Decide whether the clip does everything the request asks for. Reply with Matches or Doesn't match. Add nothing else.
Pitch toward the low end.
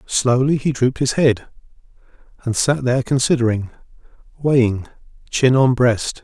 Matches